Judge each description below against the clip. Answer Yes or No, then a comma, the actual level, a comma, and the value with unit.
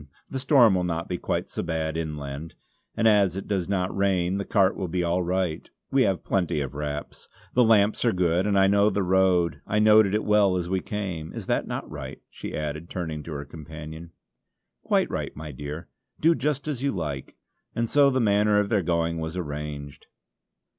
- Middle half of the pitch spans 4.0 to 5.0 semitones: Yes, average, 4.5 semitones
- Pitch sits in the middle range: No, very low, 90 Hz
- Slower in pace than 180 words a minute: No, average, 200 wpm